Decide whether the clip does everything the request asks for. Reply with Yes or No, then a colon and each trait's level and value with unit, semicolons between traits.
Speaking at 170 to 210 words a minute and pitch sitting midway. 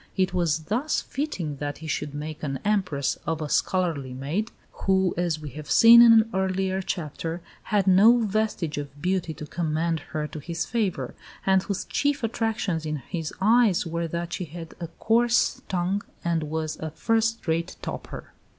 Yes: average, 175 wpm; medium, 175 Hz